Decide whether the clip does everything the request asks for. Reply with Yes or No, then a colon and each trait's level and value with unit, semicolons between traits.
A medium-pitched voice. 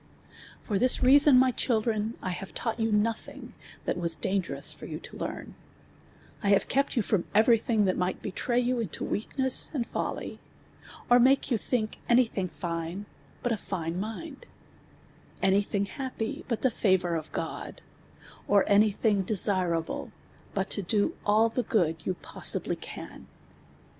No: high, 210 Hz